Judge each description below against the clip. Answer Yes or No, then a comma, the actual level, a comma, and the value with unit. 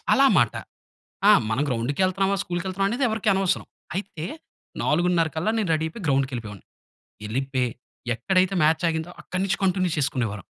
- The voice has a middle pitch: Yes, medium, 170 Hz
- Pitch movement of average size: No, wide, 6.0 semitones